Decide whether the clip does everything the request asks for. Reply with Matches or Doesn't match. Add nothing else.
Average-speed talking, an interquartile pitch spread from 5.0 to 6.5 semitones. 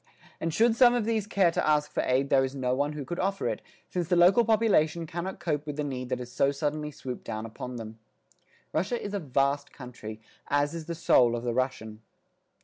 Doesn't match